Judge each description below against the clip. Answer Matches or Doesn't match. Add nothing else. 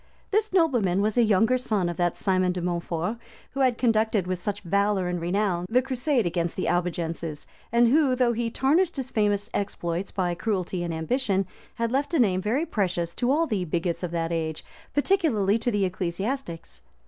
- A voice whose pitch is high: Matches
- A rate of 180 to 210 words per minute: Matches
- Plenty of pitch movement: Matches